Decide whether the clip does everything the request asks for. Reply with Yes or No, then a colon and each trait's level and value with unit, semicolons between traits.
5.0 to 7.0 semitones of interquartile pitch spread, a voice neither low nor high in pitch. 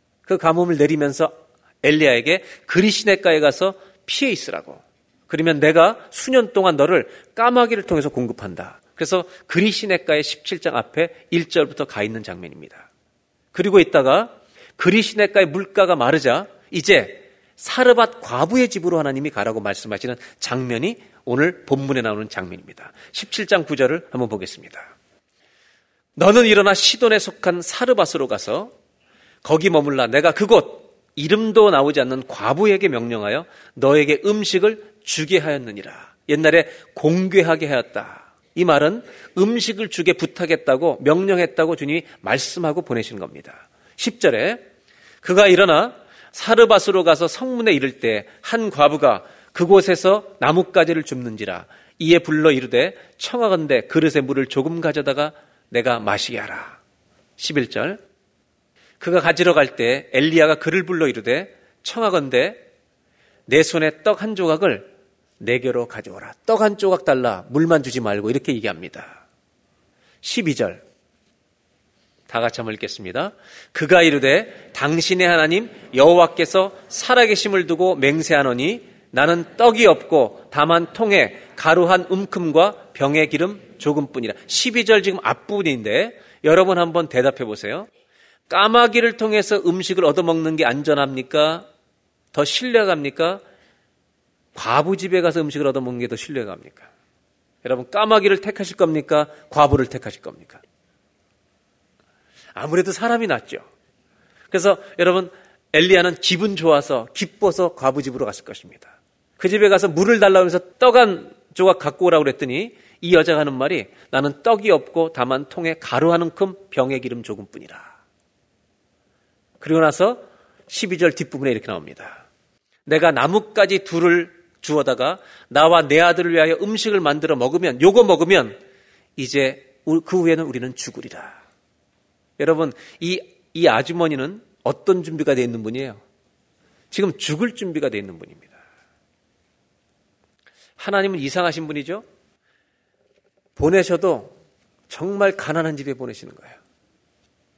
Yes: average, 5.3 semitones; medium, 165 Hz